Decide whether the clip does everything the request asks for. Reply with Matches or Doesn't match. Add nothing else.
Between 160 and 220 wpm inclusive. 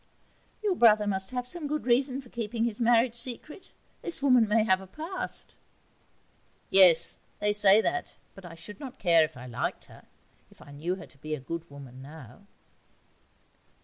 Matches